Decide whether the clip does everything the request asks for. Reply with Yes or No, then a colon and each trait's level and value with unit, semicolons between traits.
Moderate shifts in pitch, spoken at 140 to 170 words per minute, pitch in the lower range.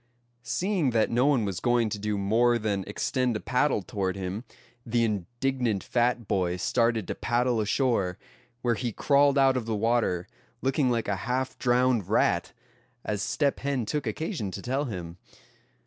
Yes: average, 3.7 semitones; average, 165 wpm; low, 120 Hz